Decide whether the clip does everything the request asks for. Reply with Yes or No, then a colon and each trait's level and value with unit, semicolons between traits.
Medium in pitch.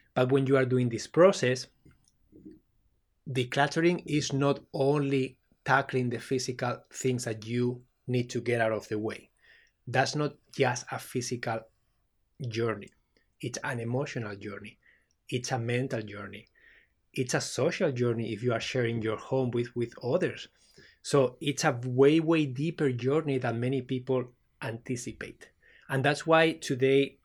No: low, 125 Hz